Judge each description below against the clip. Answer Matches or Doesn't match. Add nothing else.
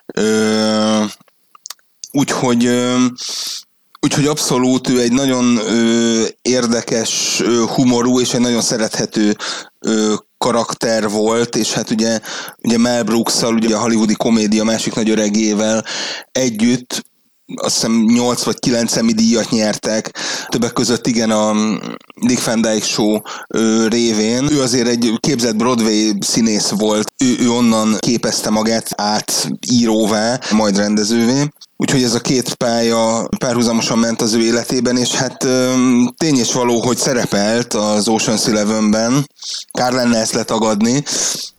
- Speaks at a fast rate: Doesn't match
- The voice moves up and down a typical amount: Doesn't match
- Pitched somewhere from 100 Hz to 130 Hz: Matches